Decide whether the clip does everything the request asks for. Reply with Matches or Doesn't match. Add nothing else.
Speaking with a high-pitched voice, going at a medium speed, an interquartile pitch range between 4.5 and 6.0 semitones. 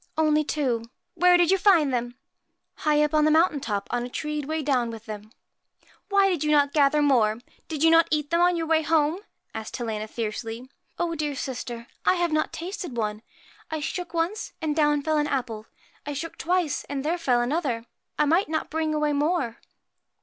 Doesn't match